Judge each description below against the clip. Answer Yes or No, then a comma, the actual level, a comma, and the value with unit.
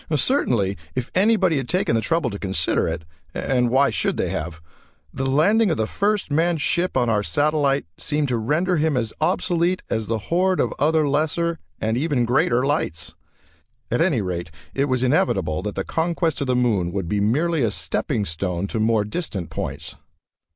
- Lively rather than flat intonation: Yes, wide, 7.6 semitones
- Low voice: Yes, low, 130 Hz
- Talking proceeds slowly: No, average, 185 wpm